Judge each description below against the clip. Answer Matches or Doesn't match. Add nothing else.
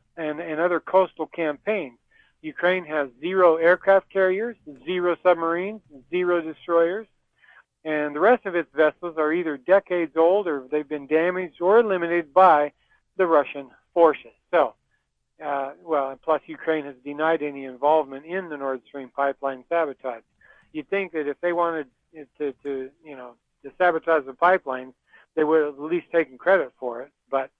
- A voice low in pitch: Doesn't match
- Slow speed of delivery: Doesn't match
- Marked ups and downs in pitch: Doesn't match